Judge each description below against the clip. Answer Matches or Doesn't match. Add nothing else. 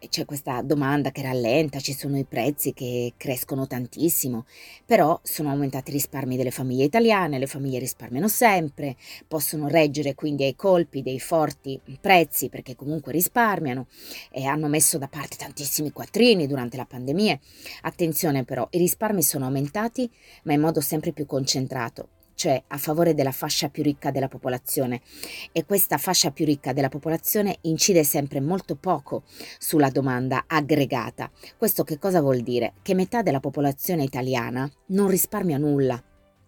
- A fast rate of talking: Doesn't match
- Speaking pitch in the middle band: Matches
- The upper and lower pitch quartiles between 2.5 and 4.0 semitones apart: Matches